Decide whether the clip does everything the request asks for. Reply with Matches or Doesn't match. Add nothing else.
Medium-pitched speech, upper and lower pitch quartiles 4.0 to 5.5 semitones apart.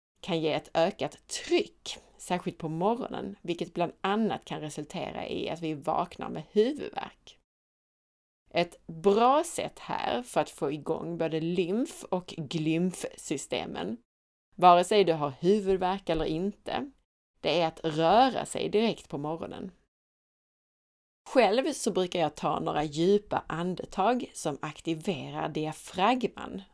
Matches